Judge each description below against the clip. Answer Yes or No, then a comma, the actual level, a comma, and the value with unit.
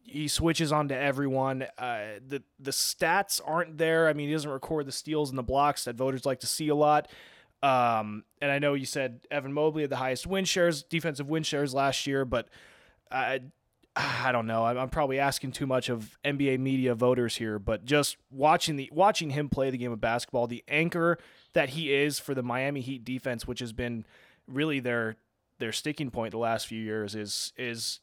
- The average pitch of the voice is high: No, low, 135 Hz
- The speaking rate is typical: No, fast, 210 wpm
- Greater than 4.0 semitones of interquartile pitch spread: No, average, 3.5 semitones